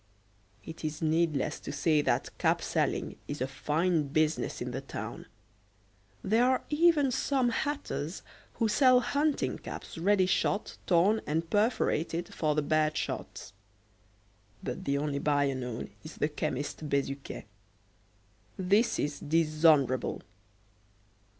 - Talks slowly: Yes, slow, 125 wpm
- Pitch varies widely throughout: Yes, wide, 6.0 semitones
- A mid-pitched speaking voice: Yes, medium, 160 Hz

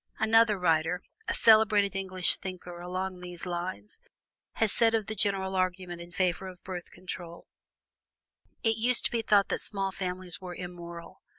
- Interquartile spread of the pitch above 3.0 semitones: No, narrow, 2.5 semitones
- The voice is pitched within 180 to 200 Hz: Yes, medium, 185 Hz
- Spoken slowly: No, average, 165 wpm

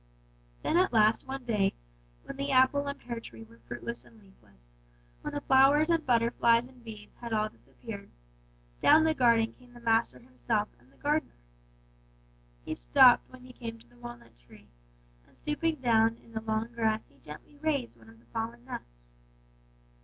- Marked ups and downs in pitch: No, average, 5.0 semitones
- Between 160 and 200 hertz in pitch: No, high, 230 Hz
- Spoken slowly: No, average, 180 wpm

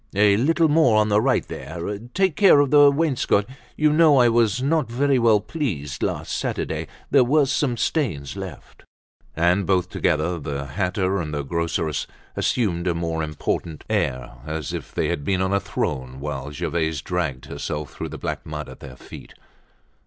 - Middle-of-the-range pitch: No, very low, 95 Hz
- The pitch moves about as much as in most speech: No, wide, 9.0 semitones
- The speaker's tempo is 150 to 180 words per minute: Yes, average, 175 wpm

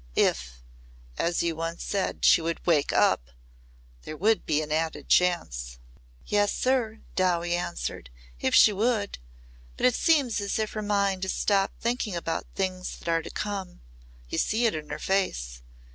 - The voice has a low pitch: No, medium, 185 Hz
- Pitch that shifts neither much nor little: Yes, average, 4.4 semitones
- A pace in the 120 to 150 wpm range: No, average, 165 wpm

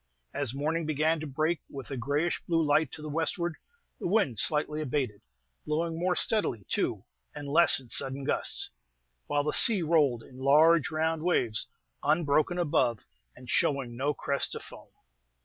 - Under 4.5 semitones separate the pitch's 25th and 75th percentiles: Yes, average, 3.1 semitones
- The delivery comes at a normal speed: Yes, average, 165 wpm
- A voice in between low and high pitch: Yes, medium, 150 Hz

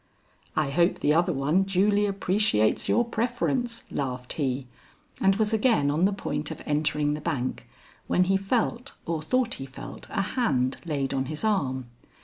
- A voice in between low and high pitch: Yes, medium, 170 Hz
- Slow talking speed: No, average, 165 wpm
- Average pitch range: No, wide, 6.7 semitones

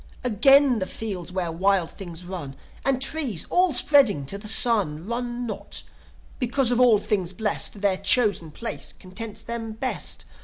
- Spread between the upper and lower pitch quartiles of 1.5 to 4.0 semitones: No, average, 4.8 semitones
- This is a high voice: Yes, high, 215 Hz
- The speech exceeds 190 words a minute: No, average, 155 wpm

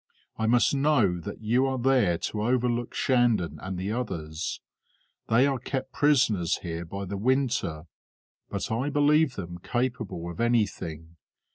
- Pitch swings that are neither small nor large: No, wide, 6.5 semitones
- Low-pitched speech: Yes, low, 115 Hz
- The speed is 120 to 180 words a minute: Yes, average, 145 wpm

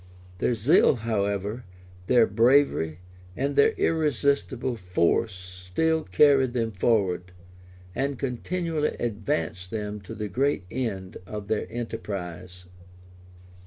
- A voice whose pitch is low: Yes, low, 110 Hz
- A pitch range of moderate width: No, wide, 6.1 semitones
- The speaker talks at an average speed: No, slow, 105 wpm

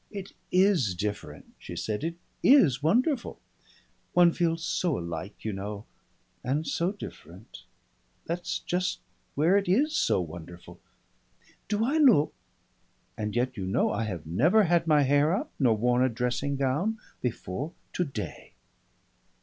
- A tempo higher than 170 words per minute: No, average, 140 wpm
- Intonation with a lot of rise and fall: Yes, wide, 9.0 semitones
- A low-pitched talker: No, medium, 145 Hz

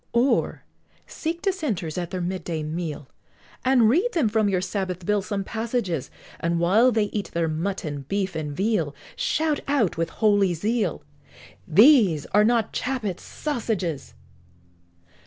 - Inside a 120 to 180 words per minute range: Yes, average, 140 wpm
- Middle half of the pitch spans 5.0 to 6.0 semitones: Yes, wide, 5.5 semitones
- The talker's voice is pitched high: Yes, high, 200 Hz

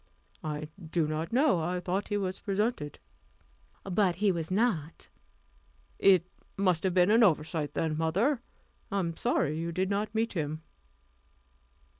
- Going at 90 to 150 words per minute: Yes, average, 145 wpm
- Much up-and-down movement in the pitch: No, average, 4.1 semitones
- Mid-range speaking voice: Yes, medium, 180 Hz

